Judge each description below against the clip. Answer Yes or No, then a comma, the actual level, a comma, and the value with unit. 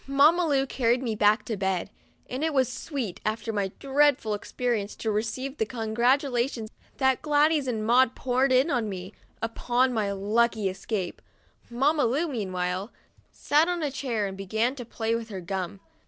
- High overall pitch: Yes, high, 235 Hz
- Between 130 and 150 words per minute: No, average, 170 wpm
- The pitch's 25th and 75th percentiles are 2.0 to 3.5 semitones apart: No, average, 4.2 semitones